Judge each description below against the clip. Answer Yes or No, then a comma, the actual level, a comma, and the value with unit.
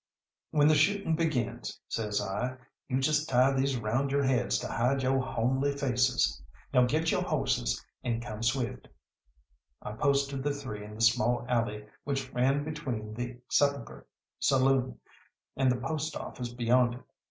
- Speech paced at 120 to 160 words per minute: Yes, average, 155 wpm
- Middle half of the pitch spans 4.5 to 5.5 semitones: No, average, 2.9 semitones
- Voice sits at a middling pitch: No, low, 130 Hz